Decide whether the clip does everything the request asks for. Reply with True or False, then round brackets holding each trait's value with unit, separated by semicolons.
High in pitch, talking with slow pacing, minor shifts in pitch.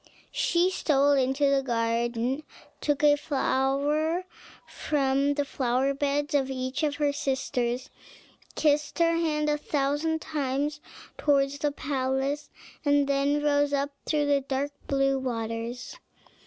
True (280 Hz; 130 wpm; 1.7 semitones)